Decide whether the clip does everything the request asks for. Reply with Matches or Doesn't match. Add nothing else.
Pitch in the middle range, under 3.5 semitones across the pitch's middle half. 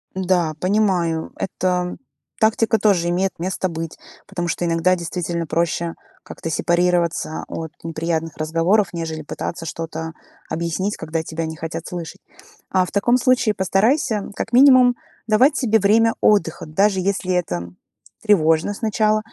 Doesn't match